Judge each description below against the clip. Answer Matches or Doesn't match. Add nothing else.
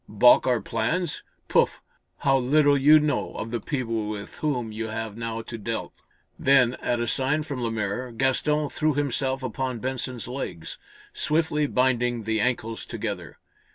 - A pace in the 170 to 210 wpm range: Doesn't match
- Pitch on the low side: Matches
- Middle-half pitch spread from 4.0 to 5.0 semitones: Doesn't match